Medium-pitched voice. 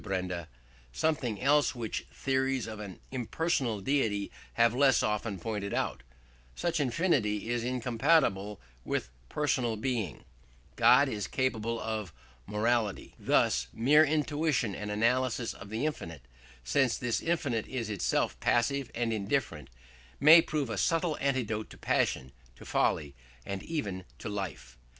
No: low, 115 Hz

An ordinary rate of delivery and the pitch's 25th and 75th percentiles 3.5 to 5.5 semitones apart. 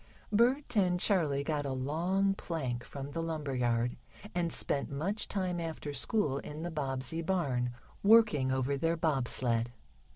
Yes: average, 155 wpm; average, 5.1 semitones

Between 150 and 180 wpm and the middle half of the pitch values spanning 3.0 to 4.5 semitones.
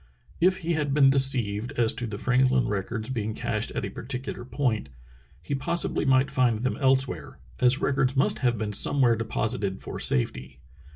Yes: average, 170 wpm; average, 3.6 semitones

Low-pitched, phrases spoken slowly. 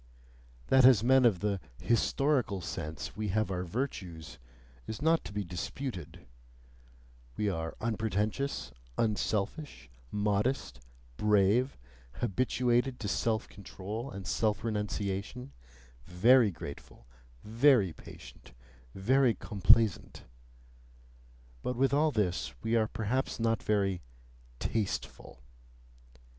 Yes: low, 105 Hz; slow, 100 wpm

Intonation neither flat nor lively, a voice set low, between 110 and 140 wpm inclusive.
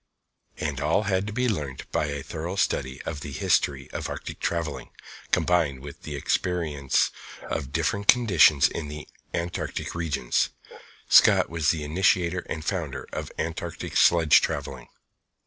Yes: average, 3.6 semitones; very low, 80 Hz; slow, 135 wpm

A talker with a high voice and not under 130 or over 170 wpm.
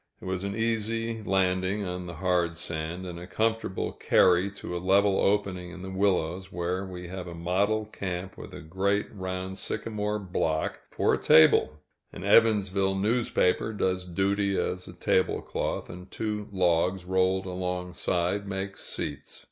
No: very low, 95 Hz; average, 155 wpm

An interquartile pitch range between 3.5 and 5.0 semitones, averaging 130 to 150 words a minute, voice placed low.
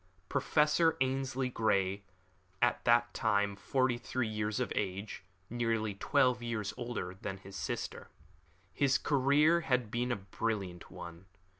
Yes: average, 4.3 semitones; slow, 135 wpm; low, 115 Hz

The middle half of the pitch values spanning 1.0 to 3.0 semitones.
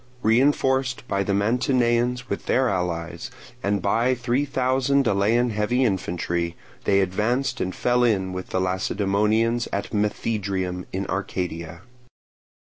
No: average, 4.7 semitones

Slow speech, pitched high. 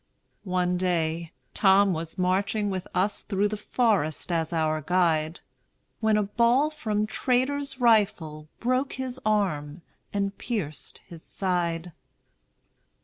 Yes: slow, 120 wpm; high, 195 Hz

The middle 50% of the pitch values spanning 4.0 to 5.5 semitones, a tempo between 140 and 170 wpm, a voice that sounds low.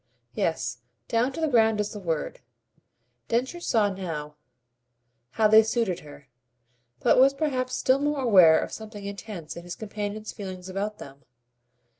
No: average, 4.5 semitones; average, 150 wpm; high, 210 Hz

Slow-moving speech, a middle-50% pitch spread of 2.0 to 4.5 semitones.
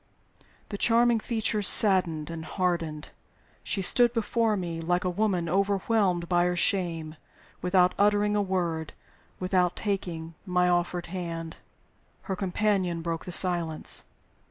Yes: slow, 125 wpm; average, 3.2 semitones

